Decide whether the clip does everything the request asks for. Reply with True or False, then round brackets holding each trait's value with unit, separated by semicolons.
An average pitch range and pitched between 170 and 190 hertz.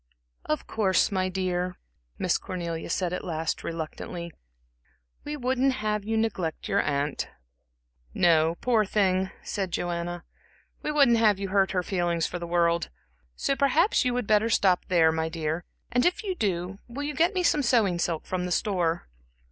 True (5.0 semitones; 185 Hz)